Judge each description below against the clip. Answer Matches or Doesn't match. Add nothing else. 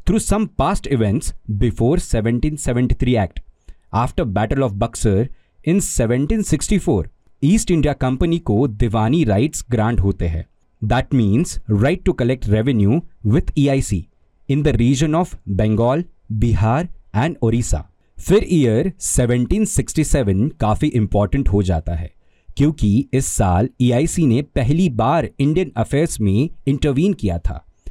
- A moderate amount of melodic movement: Doesn't match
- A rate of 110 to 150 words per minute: Matches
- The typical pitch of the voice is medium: Doesn't match